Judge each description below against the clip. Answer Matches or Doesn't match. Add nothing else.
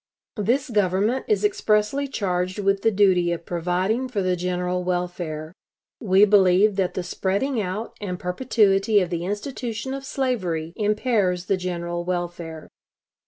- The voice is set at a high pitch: Matches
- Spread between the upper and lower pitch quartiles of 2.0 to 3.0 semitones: Doesn't match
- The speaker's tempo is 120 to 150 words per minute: Matches